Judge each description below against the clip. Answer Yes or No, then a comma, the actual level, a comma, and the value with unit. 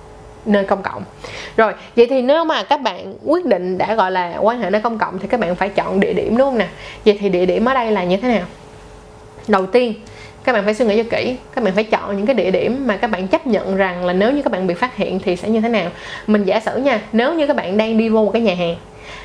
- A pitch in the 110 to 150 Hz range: No, high, 215 Hz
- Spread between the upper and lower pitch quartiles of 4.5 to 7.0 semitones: No, average, 4.0 semitones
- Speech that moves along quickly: Yes, fast, 285 wpm